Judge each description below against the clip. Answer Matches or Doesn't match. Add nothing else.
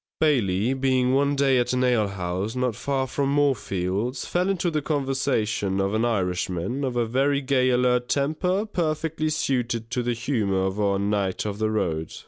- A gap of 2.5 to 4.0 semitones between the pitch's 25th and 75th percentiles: Doesn't match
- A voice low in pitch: Matches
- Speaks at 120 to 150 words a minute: Doesn't match